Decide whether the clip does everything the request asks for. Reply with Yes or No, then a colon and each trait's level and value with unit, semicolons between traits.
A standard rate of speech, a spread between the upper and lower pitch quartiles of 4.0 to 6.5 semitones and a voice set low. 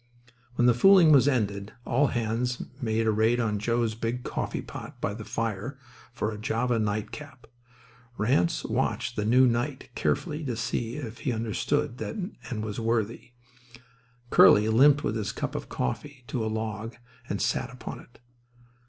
No: average, 160 wpm; average, 2.9 semitones; low, 115 Hz